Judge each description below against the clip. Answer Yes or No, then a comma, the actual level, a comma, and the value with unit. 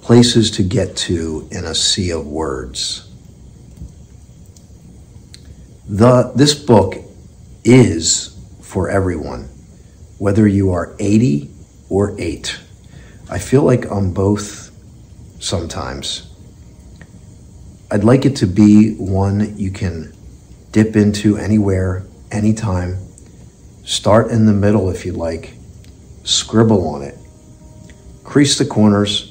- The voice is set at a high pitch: No, low, 100 Hz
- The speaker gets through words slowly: Yes, slow, 105 wpm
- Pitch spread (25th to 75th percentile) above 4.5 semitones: No, average, 3.2 semitones